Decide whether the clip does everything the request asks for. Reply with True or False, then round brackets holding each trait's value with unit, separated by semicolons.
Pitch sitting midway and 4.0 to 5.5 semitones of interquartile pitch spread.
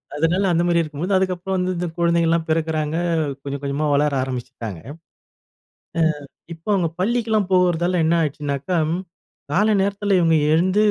False (170 Hz; 3.4 semitones)